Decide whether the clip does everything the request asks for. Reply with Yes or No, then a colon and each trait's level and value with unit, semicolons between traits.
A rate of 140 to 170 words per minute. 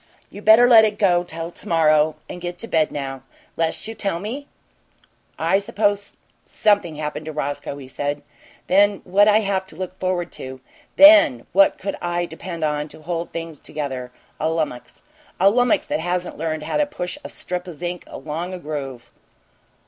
No: average, 180 wpm